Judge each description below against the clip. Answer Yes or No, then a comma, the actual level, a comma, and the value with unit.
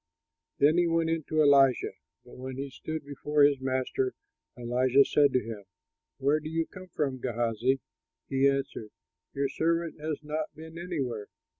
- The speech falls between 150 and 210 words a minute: Yes, average, 160 wpm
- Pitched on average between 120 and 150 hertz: Yes, medium, 140 Hz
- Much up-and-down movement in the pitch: No, average, 3.3 semitones